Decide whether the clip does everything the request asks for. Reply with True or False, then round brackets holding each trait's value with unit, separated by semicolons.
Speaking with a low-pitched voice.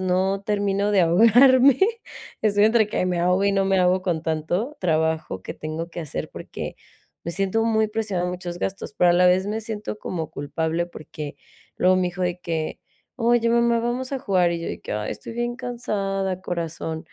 False (185 Hz)